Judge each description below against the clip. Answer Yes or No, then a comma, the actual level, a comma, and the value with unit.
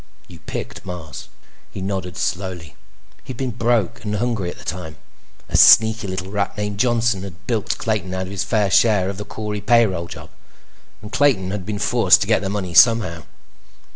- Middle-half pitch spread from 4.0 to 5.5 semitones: No, average, 3.1 semitones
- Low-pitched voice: Yes, low, 100 Hz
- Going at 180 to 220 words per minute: Yes, average, 185 wpm